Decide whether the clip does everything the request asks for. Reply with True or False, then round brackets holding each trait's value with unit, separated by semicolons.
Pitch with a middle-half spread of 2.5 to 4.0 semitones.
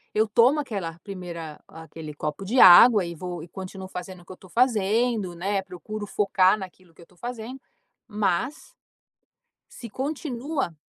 False (4.8 semitones)